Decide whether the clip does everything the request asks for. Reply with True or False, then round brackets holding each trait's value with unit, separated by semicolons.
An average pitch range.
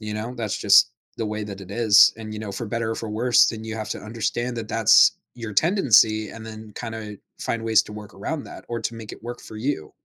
False (1.5 semitones)